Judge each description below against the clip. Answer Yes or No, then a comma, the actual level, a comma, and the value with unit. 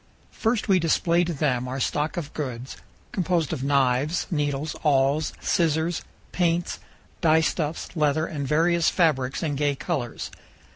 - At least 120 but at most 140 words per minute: Yes, slow, 135 wpm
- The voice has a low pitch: No, medium, 155 Hz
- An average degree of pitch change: Yes, average, 3.3 semitones